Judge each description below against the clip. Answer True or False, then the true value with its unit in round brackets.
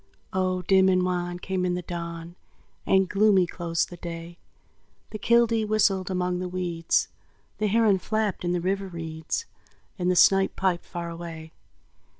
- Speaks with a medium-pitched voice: True (180 Hz)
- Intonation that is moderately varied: False (2.0 semitones)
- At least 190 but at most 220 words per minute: False (155 wpm)